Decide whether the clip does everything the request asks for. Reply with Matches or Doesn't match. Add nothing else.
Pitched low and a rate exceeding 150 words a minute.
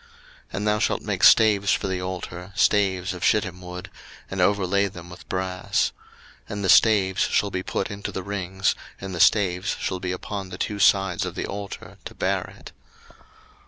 Matches